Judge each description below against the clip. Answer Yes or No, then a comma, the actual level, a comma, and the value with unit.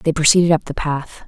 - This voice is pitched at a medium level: Yes, medium, 155 Hz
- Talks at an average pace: No, fast, 235 wpm